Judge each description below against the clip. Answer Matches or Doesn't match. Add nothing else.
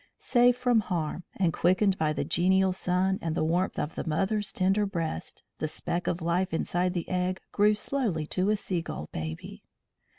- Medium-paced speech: Matches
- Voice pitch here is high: Doesn't match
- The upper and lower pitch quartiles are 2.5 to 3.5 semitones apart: Matches